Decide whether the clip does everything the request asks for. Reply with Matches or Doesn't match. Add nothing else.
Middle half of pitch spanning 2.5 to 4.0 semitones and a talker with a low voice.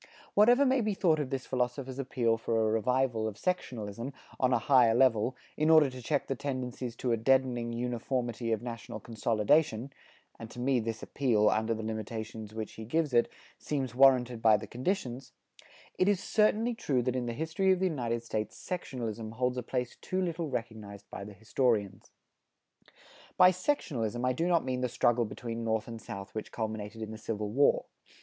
Matches